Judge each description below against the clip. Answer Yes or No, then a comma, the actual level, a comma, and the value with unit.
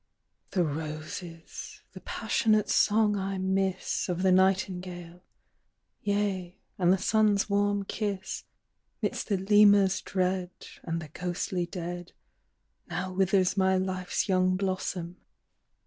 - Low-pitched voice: No, medium, 185 Hz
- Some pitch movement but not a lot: No, narrow, 1.8 semitones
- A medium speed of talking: No, slow, 115 wpm